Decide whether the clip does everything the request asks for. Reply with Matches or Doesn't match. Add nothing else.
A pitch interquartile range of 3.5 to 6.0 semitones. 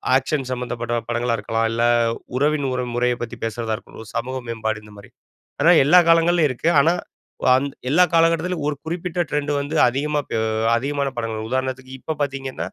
Matches